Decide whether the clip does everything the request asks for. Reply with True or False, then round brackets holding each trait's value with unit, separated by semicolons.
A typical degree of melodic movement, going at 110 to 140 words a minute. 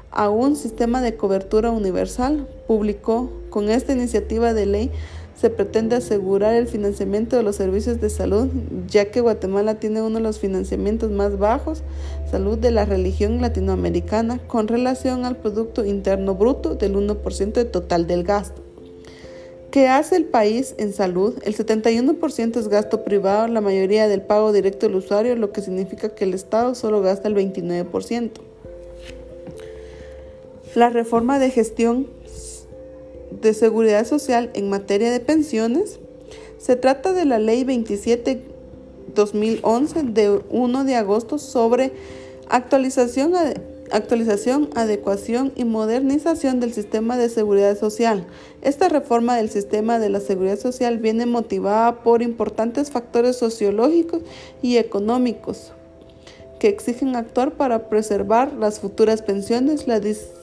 True (3.4 semitones; 135 wpm)